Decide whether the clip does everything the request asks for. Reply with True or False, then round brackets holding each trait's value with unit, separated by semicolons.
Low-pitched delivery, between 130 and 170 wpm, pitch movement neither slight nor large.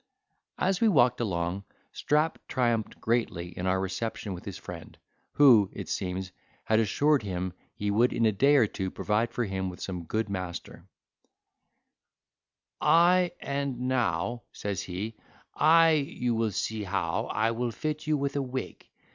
False (115 Hz; 155 wpm; 6.5 semitones)